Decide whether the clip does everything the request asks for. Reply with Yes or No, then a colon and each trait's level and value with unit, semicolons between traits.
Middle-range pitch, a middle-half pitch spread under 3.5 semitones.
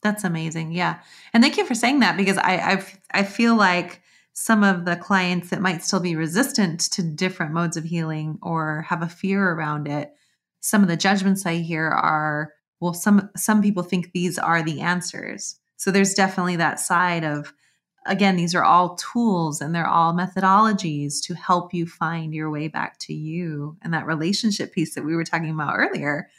Yes: medium, 175 Hz; average, 3.1 semitones